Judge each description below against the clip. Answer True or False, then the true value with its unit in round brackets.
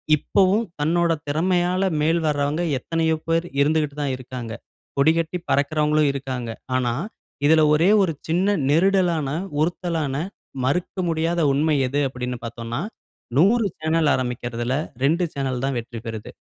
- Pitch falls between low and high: True (150 Hz)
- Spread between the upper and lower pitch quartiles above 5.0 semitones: False (4.2 semitones)